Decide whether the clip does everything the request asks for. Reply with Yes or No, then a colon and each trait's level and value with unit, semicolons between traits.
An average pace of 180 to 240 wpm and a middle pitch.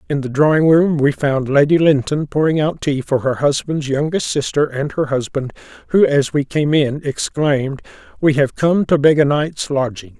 Yes: average, 195 wpm; medium, 145 Hz